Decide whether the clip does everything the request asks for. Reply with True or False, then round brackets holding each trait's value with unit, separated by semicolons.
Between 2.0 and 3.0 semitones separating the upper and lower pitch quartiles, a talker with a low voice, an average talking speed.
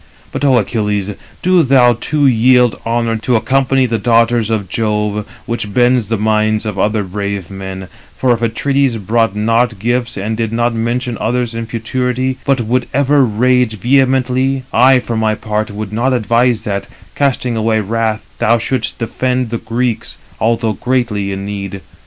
True (2.7 semitones; 115 Hz; 165 wpm)